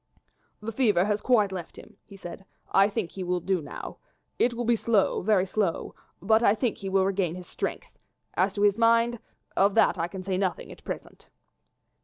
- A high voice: Yes, high, 200 Hz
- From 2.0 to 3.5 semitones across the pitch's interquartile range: Yes, average, 3.0 semitones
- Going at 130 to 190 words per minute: No, average, 200 wpm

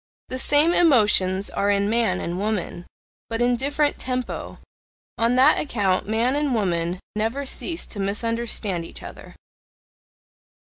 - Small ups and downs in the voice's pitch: No, average, 4.6 semitones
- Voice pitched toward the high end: Yes, high, 225 Hz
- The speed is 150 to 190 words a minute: No, slow, 135 wpm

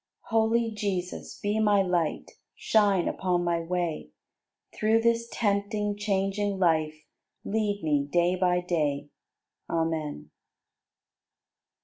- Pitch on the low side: No, medium, 185 Hz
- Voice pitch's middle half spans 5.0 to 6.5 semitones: No, average, 3.9 semitones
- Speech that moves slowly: Yes, slow, 105 wpm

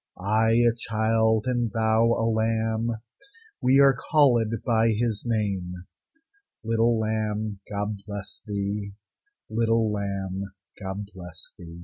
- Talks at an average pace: No, slow, 115 wpm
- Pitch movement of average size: No, narrow, 2.1 semitones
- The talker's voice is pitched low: Yes, low, 110 Hz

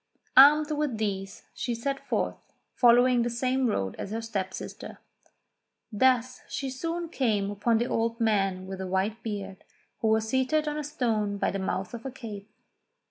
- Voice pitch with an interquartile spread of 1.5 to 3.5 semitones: No, average, 4.4 semitones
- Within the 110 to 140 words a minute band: No, average, 175 wpm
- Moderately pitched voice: No, high, 230 Hz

